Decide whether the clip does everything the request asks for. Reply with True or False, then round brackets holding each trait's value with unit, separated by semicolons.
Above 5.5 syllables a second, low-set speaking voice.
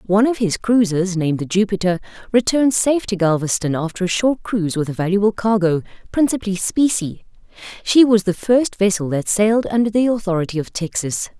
False (5.8 syllables/s; 200 Hz)